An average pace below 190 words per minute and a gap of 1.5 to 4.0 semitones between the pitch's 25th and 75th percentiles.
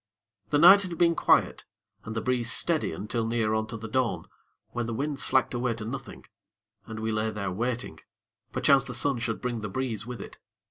No: average, 200 wpm; average, 2.9 semitones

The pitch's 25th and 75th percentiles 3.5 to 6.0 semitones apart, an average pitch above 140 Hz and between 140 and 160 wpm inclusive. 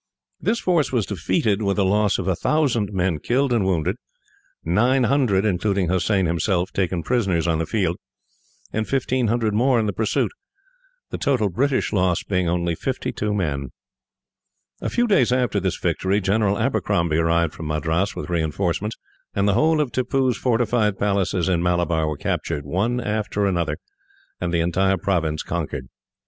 No: average, 4.6 semitones; very low, 95 Hz; average, 155 wpm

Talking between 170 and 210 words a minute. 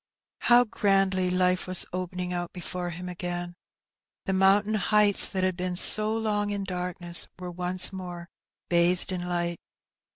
No: average, 155 wpm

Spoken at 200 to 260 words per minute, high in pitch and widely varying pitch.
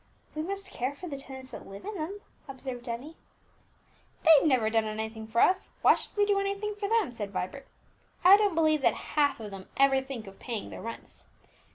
Yes: fast, 205 wpm; very high, 275 Hz; wide, 8.1 semitones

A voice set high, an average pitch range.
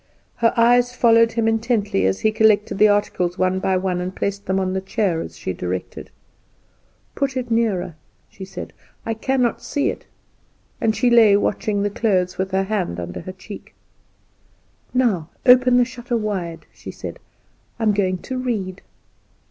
Yes: high, 205 Hz; average, 3.9 semitones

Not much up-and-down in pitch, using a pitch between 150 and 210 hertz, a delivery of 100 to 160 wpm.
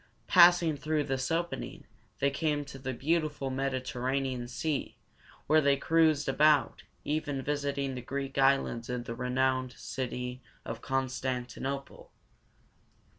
No: narrow, 2.3 semitones; low, 135 Hz; average, 150 wpm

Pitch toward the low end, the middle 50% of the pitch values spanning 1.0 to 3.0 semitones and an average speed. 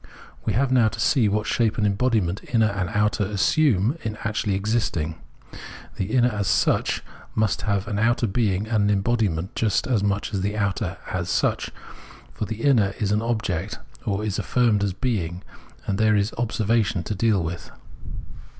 Yes: low, 105 Hz; narrow, 2.6 semitones; average, 175 wpm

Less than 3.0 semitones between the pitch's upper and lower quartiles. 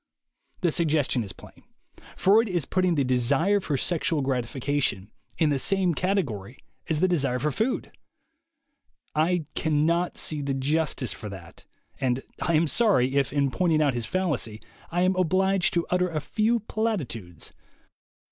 No: wide, 5.6 semitones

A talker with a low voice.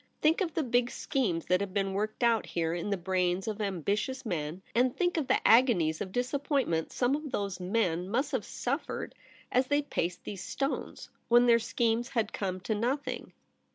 No: high, 225 Hz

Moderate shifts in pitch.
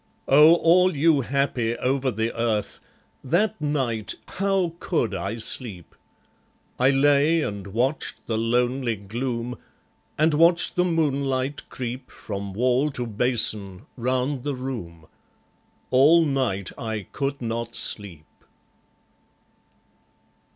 Yes: average, 4.3 semitones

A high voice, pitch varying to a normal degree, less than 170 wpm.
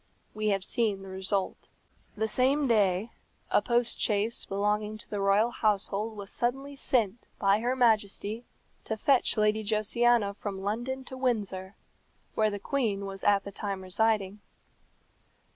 Yes: high, 215 Hz; average, 3.0 semitones; average, 145 wpm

